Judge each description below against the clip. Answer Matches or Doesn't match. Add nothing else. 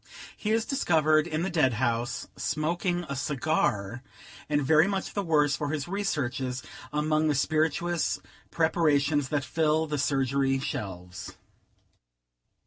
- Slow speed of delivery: Matches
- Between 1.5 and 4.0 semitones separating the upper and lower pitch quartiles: Matches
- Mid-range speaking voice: Matches